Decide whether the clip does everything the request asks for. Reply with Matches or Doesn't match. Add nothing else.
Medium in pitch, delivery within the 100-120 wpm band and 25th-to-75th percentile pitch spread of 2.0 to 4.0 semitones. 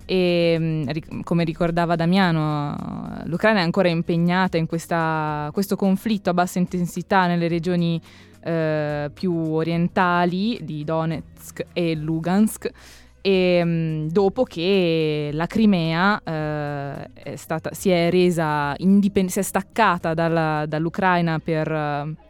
Matches